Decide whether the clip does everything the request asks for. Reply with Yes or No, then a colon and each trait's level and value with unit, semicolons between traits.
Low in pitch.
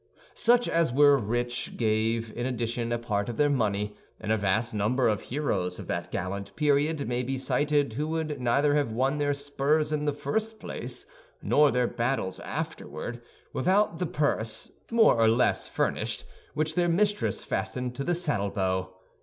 Yes: low, 125 Hz